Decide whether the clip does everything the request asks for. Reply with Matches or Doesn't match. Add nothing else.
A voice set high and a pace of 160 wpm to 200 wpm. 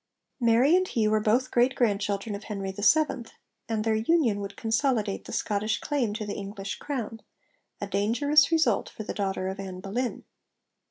Matches